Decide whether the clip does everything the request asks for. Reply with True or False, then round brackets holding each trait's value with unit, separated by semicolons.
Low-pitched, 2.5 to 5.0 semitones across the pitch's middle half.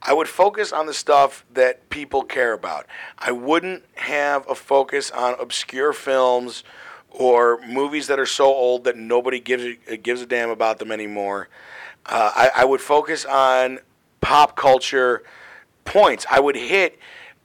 True (130 Hz; 2.9 semitones)